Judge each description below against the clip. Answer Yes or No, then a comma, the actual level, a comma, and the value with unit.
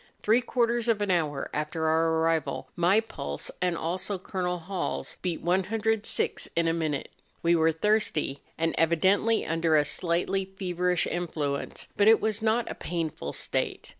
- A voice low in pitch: No, medium, 175 Hz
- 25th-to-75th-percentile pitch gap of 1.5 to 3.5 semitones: No, average, 4.0 semitones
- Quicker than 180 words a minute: No, average, 155 wpm